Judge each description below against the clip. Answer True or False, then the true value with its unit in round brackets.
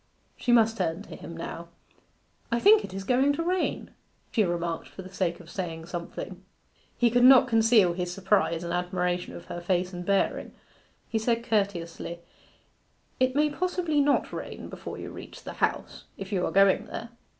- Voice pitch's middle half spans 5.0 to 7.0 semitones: True (5.6 semitones)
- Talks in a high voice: True (195 Hz)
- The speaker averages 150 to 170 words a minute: False (180 wpm)